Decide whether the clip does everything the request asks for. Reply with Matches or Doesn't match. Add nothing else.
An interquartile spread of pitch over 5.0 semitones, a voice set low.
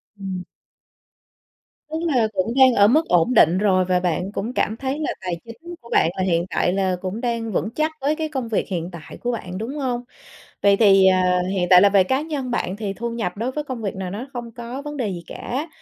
Doesn't match